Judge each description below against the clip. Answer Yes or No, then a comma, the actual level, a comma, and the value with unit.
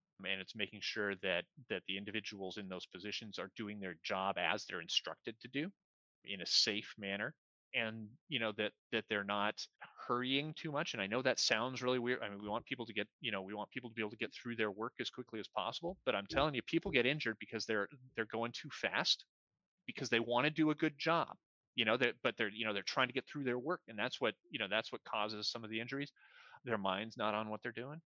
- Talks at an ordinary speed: No, fast, 255 wpm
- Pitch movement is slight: No, average, 3.3 semitones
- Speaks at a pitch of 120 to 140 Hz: No, low, 110 Hz